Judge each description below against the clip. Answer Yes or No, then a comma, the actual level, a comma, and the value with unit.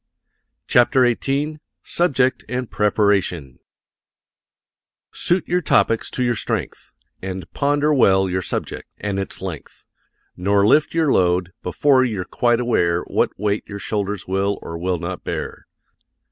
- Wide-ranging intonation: Yes, wide, 5.7 semitones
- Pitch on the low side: Yes, low, 105 Hz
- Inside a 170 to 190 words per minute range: No, slow, 135 wpm